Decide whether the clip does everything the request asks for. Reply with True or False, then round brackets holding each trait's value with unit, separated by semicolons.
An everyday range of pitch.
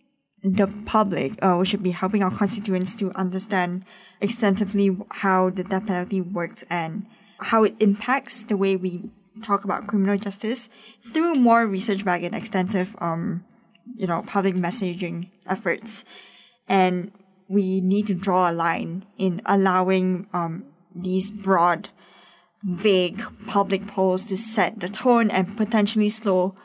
False (2.3 semitones)